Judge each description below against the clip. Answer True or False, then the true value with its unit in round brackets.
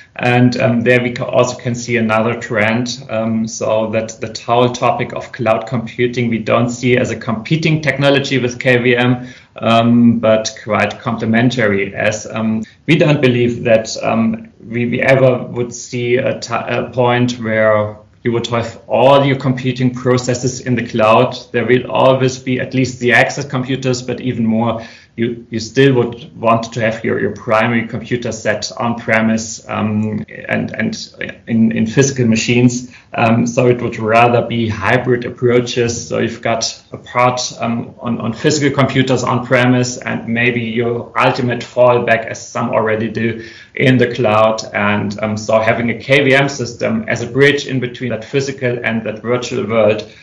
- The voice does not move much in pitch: True (1.8 semitones)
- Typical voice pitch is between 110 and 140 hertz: True (120 Hz)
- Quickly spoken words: False (170 wpm)